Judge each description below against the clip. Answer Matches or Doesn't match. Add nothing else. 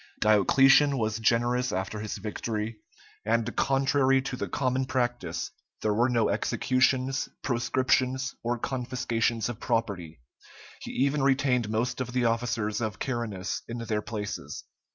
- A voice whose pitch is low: Matches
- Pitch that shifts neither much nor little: Matches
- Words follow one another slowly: Matches